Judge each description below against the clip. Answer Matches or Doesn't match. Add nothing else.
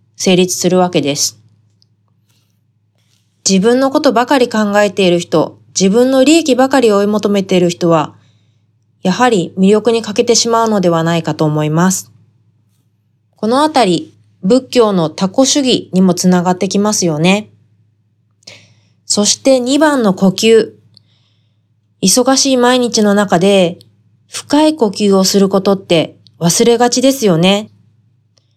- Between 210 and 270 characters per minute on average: Matches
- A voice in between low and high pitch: Matches